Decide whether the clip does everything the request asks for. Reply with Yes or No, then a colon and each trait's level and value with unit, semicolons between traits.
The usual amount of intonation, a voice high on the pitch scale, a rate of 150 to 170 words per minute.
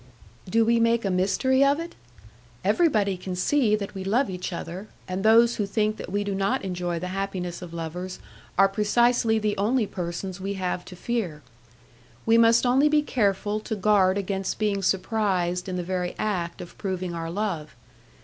No: average, 3.4 semitones; high, 195 Hz; average, 180 wpm